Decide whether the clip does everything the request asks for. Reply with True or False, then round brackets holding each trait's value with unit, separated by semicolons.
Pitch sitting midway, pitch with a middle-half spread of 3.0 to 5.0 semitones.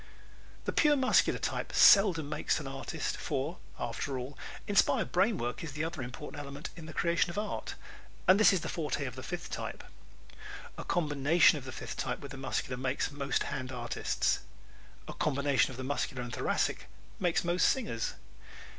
True (145 Hz; 4.7 semitones)